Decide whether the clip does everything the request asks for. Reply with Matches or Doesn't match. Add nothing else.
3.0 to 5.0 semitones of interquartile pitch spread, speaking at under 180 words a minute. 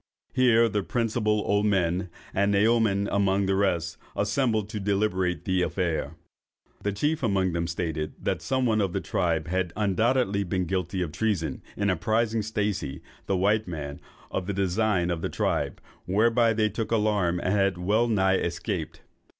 Matches